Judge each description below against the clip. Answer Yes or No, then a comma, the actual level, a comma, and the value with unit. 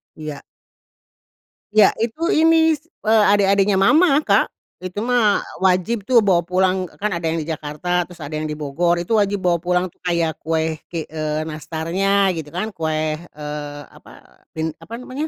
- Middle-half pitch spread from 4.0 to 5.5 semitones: Yes, average, 4.7 semitones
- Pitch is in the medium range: Yes, medium, 180 Hz